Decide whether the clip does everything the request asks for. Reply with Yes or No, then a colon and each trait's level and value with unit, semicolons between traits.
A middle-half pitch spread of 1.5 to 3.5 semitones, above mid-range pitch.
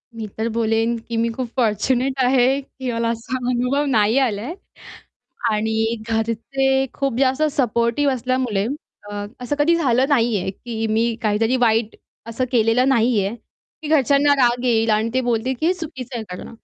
Yes: average, 2.8 semitones; high, 240 Hz